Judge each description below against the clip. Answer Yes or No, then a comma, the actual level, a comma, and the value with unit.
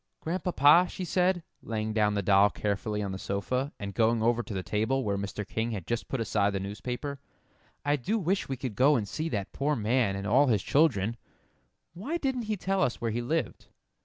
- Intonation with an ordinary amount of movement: No, wide, 6.5 semitones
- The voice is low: Yes, low, 120 Hz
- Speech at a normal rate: No, fast, 210 wpm